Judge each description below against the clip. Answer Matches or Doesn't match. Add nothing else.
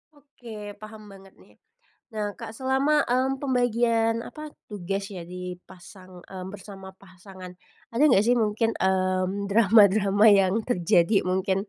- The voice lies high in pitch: Matches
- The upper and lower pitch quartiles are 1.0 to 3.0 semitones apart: Doesn't match